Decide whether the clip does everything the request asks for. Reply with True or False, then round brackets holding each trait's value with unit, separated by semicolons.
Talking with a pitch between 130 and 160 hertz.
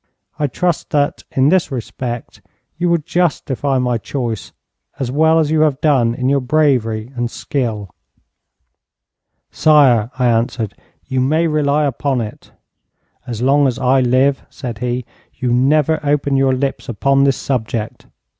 True (135 Hz)